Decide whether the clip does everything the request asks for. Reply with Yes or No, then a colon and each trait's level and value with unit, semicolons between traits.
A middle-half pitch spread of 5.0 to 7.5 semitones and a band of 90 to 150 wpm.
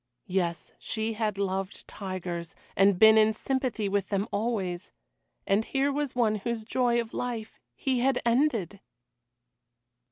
No: average, 3.7 semitones; slow, 135 wpm